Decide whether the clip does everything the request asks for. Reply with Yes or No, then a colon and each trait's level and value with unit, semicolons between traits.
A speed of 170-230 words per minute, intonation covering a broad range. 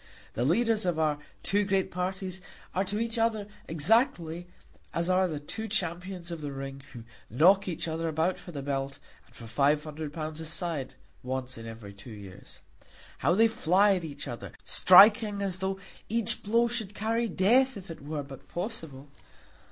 Yes: average, 180 wpm; wide, 5.8 semitones